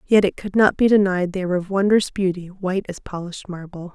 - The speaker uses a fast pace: Yes, fast, 230 wpm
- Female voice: Yes, female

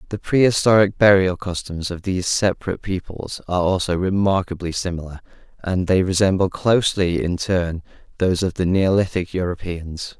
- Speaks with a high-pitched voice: No, very low, 90 Hz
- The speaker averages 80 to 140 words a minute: Yes, slow, 135 wpm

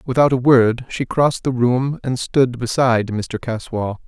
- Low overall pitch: Yes, low, 125 Hz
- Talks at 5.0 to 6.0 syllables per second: No, 4.4 syllables/s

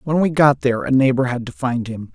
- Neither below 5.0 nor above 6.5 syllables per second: Yes, 5.9 syllables/s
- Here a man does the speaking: Yes, male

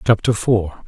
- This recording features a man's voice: Yes, male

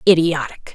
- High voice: No, medium, 160 Hz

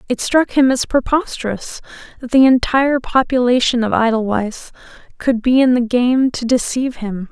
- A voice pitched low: No, high, 245 Hz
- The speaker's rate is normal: Yes, average, 155 wpm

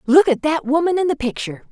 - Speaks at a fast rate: Yes, fast, 245 wpm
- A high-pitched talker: Yes, very high, 295 Hz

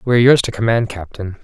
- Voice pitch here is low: Yes, low, 110 Hz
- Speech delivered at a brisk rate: Yes, fast, 210 wpm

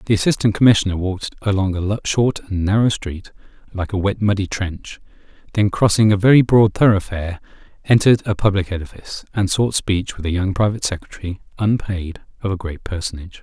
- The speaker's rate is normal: Yes, average, 170 wpm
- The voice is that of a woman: No, male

